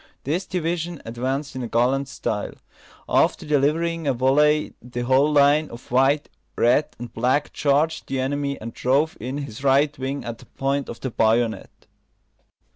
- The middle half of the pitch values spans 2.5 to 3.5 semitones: Yes, average, 3.2 semitones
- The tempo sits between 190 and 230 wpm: No, average, 155 wpm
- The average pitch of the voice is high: No, low, 135 Hz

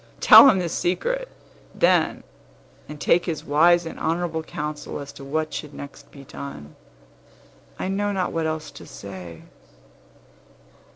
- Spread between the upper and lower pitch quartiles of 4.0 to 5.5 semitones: No, average, 3.6 semitones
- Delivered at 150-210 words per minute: No, average, 140 wpm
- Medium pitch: Yes, medium, 155 Hz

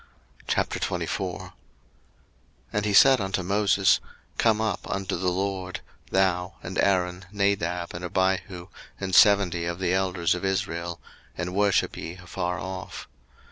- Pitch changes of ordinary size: No, narrow, 1.8 semitones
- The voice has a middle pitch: No, very low, 95 Hz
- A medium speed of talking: No, slow, 130 wpm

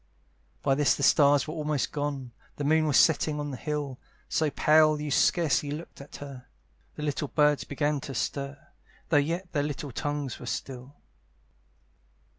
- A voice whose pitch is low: No, medium, 145 Hz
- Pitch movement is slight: Yes, narrow, 1.5 semitones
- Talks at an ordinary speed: Yes, average, 160 wpm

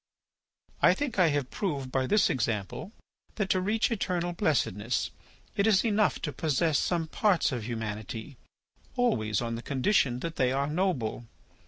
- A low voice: No, medium, 145 Hz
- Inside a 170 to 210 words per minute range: No, average, 155 wpm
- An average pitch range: No, wide, 7.8 semitones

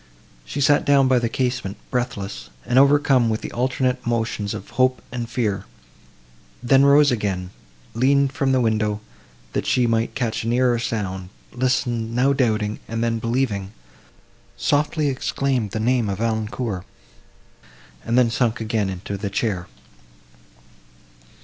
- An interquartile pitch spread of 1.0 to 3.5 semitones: Yes, average, 3.2 semitones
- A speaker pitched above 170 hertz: No, low, 120 Hz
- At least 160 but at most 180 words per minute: No, average, 140 wpm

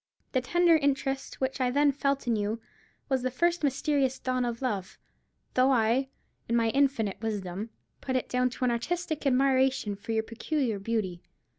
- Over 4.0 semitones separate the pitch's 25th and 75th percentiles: No, average, 3.4 semitones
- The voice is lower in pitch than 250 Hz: No, very high, 255 Hz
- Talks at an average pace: Yes, average, 170 wpm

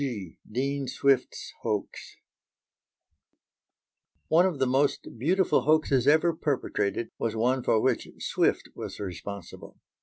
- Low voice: Yes, low, 130 Hz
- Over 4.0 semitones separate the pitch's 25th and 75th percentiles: Yes, average, 4.5 semitones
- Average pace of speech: No, slow, 115 wpm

